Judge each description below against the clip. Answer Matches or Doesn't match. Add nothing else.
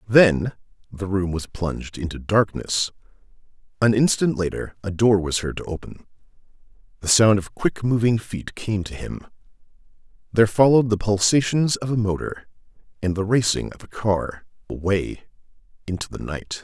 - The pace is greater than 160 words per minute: Doesn't match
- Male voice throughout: Matches